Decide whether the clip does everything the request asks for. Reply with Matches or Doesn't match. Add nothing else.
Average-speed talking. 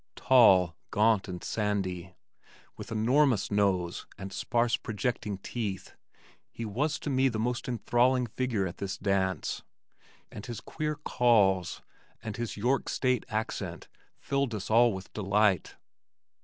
Doesn't match